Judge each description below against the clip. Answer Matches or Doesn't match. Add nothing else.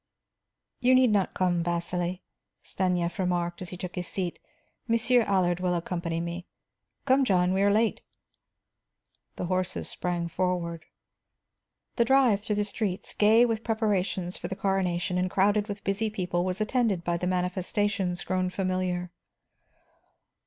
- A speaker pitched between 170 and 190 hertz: Matches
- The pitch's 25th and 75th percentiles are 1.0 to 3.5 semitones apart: Matches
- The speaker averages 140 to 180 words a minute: Matches